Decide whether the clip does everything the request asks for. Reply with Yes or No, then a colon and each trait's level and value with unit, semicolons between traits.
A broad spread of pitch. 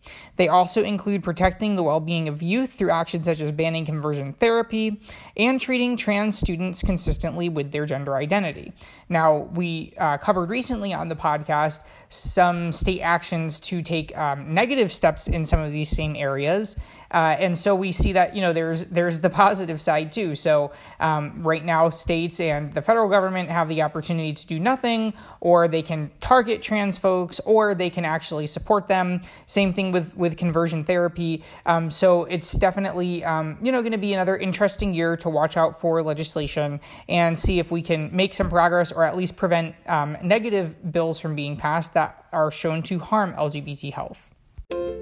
No: average, 3.3 semitones